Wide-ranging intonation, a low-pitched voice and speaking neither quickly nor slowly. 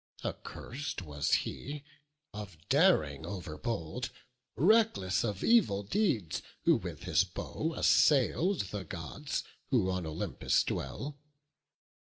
No: wide, 8.9 semitones; low, 105 Hz; slow, 110 wpm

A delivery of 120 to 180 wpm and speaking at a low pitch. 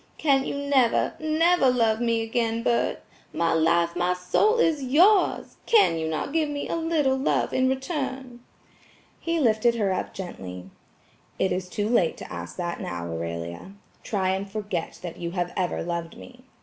No: average, 170 wpm; high, 220 Hz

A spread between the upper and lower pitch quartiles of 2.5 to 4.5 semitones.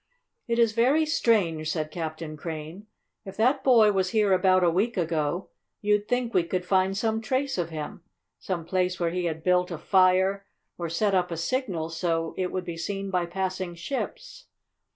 Yes: average, 4.1 semitones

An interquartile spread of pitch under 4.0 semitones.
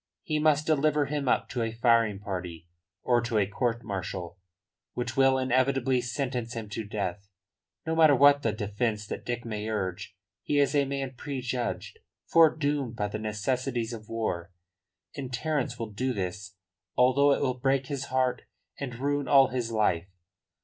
No: average, 4.3 semitones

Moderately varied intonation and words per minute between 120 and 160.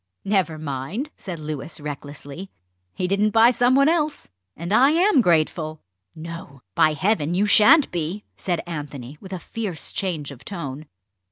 No: wide, 5.7 semitones; average, 155 wpm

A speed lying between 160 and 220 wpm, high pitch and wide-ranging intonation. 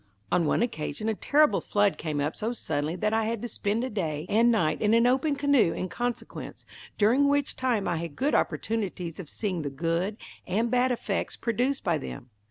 Yes: average, 200 wpm; high, 210 Hz; wide, 6.3 semitones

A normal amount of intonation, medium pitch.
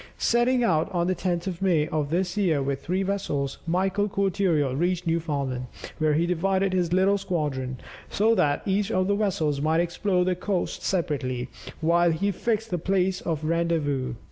Yes: average, 3.9 semitones; medium, 175 Hz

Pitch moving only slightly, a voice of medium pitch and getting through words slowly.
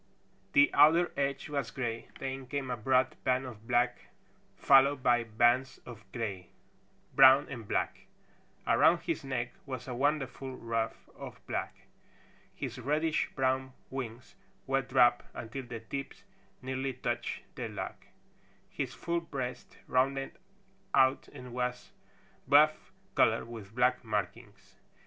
No: narrow, 2.2 semitones; low, 130 Hz; slow, 130 wpm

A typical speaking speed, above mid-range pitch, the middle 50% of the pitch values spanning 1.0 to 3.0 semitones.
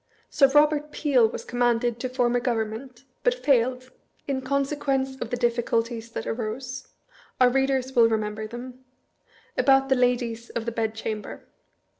Yes: average, 145 wpm; high, 245 Hz; narrow, 2.5 semitones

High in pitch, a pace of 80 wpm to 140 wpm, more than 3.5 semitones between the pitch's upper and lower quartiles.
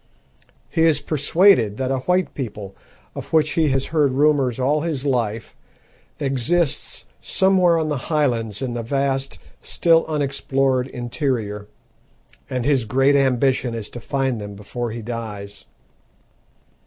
No: low, 135 Hz; slow, 135 wpm; average, 4.0 semitones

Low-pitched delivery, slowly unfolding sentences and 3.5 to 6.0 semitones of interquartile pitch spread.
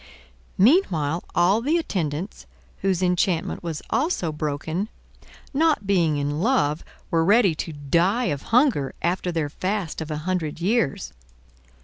No: medium, 175 Hz; slow, 130 wpm; average, 5.1 semitones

